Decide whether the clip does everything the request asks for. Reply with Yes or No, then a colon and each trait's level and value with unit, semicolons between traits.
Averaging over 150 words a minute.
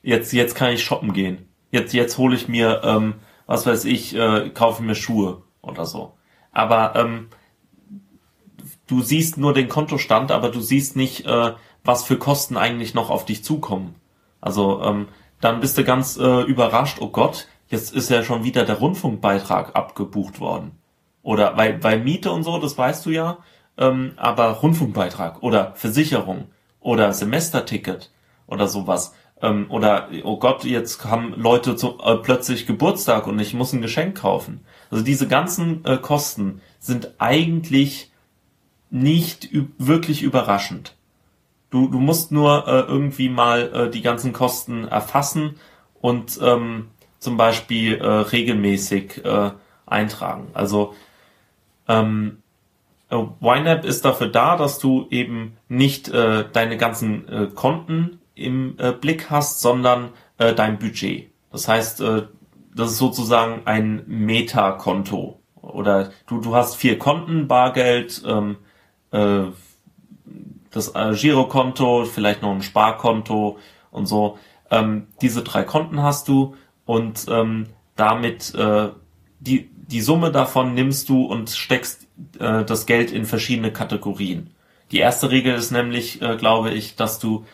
No: average, 145 wpm